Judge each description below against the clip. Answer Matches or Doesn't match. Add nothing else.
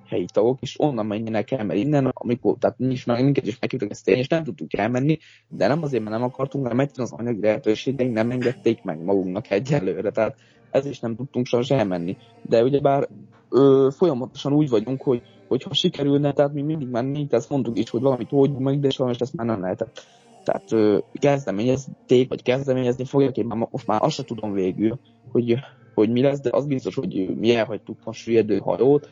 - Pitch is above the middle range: Doesn't match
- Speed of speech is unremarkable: Doesn't match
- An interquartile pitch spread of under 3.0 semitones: Doesn't match